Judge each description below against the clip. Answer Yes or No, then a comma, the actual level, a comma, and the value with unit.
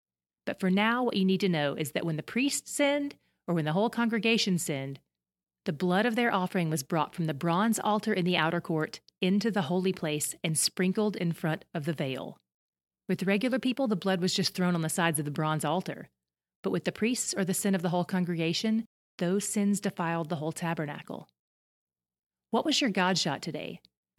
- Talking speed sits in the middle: No, fast, 210 wpm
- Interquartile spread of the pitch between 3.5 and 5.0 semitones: Yes, average, 4.4 semitones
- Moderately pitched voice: Yes, medium, 180 Hz